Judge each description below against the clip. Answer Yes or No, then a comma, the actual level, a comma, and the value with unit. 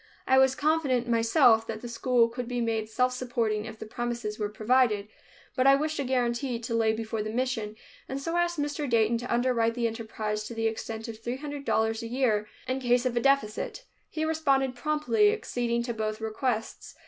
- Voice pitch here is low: No, high, 240 Hz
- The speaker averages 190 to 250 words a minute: Yes, average, 200 wpm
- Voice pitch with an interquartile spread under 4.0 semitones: Yes, average, 3.0 semitones